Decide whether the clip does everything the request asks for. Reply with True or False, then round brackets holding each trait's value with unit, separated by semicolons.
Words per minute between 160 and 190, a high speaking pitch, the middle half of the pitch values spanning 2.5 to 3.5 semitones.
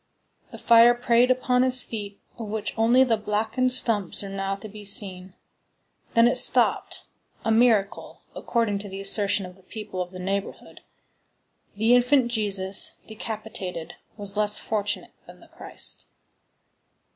False (145 wpm; 210 Hz; 3.0 semitones)